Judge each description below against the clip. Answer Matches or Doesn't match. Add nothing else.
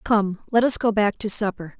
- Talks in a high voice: Matches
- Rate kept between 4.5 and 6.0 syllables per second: Matches